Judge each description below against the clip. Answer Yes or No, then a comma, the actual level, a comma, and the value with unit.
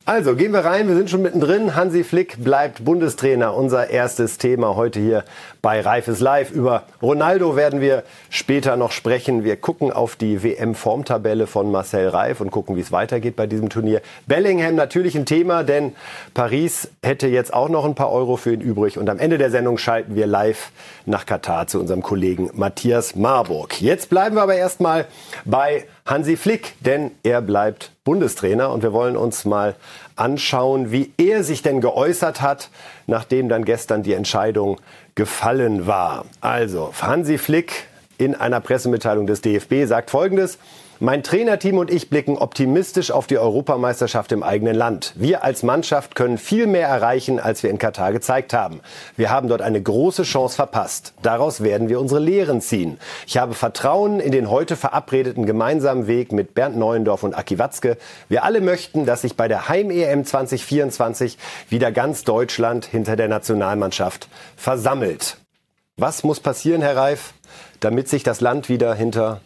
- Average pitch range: Yes, average, 4.7 semitones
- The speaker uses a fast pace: No, average, 170 wpm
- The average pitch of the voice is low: Yes, low, 125 Hz